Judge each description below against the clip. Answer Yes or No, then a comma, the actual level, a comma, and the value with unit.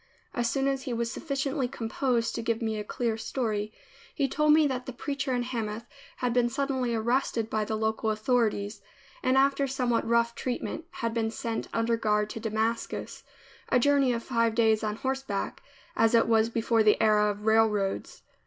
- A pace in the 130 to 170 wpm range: No, average, 180 wpm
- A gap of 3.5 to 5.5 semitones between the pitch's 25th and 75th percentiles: No, average, 2.8 semitones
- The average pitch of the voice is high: Yes, high, 230 Hz